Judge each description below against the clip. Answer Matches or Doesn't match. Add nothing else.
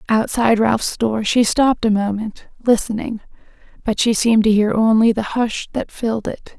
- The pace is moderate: Matches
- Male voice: Doesn't match